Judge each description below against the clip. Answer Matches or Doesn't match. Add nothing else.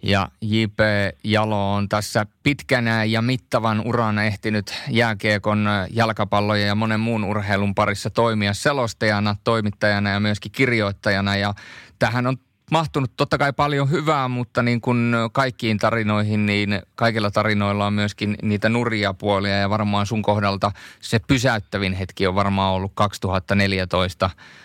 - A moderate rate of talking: Matches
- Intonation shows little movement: Matches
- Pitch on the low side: Matches